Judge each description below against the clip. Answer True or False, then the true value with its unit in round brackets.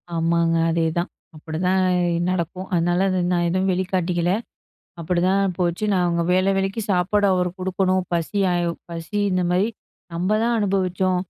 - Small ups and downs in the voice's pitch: True (1.8 semitones)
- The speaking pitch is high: False (180 Hz)